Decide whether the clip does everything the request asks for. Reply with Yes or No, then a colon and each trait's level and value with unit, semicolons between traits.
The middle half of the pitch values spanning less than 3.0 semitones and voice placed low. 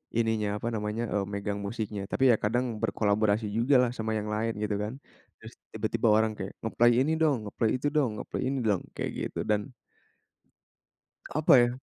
Yes: narrow, 2.5 semitones; low, 110 Hz